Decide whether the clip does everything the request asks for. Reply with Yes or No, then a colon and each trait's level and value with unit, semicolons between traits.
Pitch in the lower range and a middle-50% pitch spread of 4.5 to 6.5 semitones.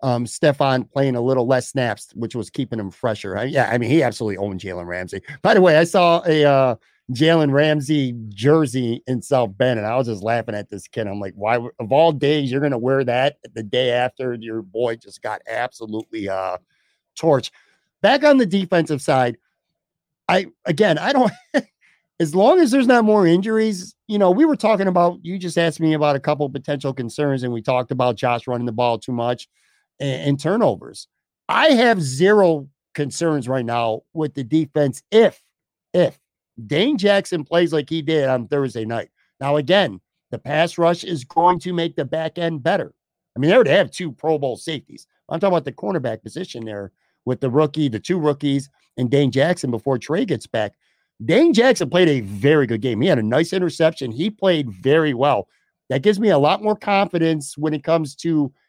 No: medium, 145 Hz; wide, 5.5 semitones